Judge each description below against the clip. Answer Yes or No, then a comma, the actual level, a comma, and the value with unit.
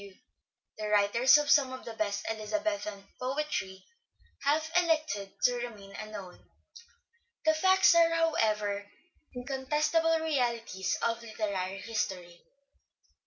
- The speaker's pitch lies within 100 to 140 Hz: No, high, 235 Hz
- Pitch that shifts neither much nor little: No, wide, 7.0 semitones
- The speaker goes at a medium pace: No, slow, 110 wpm